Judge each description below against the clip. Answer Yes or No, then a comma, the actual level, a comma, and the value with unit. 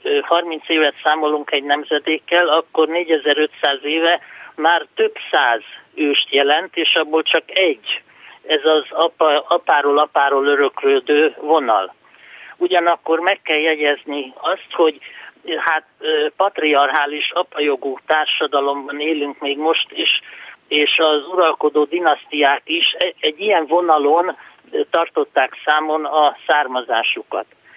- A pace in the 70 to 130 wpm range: Yes, average, 110 wpm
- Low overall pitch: No, medium, 155 Hz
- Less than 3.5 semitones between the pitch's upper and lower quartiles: Yes, average, 2.7 semitones